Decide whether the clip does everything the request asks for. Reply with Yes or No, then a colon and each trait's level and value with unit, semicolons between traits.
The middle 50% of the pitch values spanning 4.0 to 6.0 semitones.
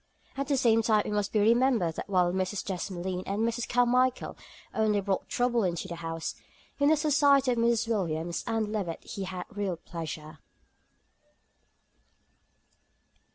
Yes: average, 4.9 semitones